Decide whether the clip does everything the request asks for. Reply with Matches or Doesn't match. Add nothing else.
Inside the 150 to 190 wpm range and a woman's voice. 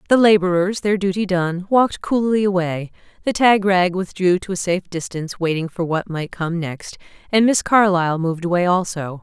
Matches